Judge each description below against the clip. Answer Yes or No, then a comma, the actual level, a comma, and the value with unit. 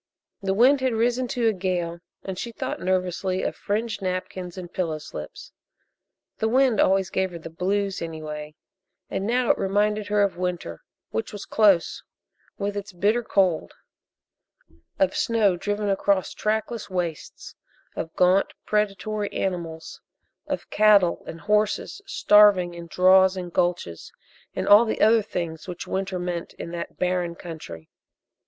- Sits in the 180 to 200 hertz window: Yes, high, 190 Hz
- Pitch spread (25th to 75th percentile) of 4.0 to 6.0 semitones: No, average, 3.2 semitones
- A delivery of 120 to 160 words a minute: Yes, average, 150 wpm